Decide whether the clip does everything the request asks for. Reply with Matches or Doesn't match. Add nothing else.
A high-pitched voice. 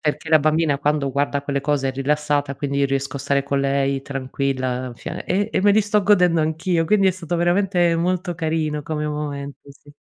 Doesn't match